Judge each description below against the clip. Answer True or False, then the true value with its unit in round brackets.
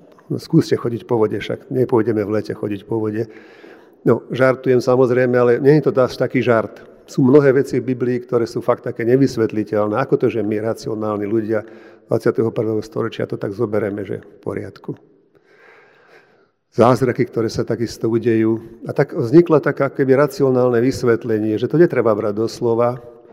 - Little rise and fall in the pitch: False (3.1 semitones)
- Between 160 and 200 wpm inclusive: True (165 wpm)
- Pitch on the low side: True (120 Hz)